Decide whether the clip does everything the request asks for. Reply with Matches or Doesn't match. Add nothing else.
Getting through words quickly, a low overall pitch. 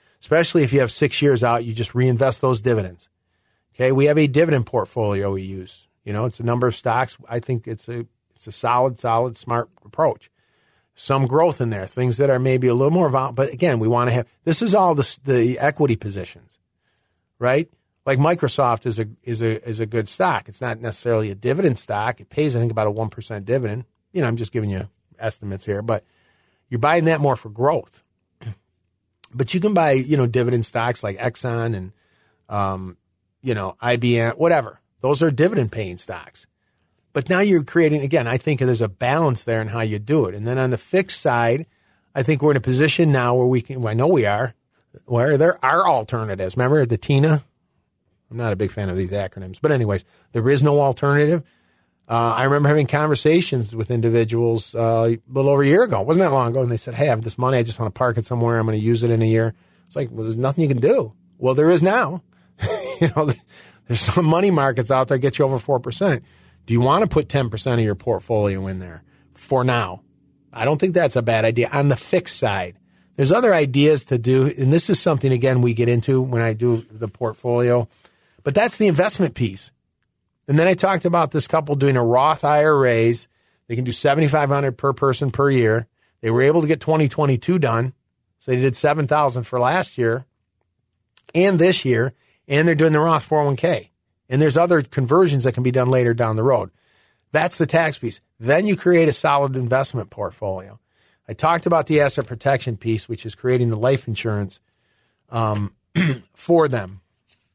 Matches